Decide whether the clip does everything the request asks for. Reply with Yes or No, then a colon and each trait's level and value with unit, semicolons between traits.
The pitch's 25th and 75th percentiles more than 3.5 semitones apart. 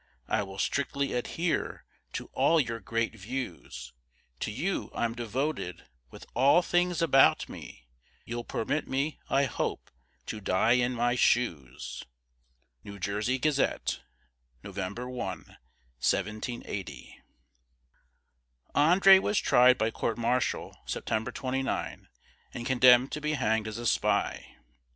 Yes: average, 4.3 semitones